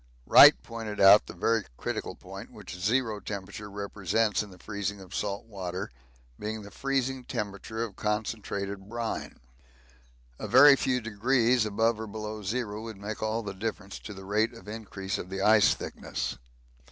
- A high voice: No, low, 105 Hz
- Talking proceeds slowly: No, average, 165 wpm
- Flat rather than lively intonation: Yes, narrow, 2.2 semitones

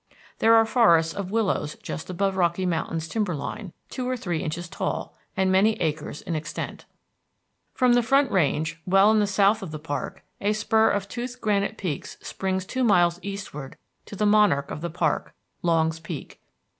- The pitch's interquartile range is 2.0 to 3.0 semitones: No, average, 4.6 semitones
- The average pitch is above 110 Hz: Yes, high, 190 Hz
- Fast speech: No, average, 180 wpm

